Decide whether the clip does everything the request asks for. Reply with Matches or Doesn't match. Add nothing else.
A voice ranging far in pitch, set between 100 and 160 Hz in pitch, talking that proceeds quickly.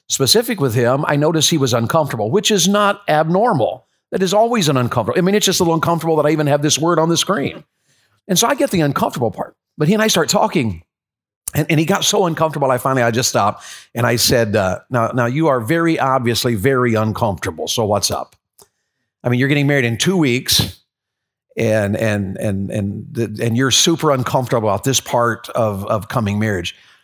Matches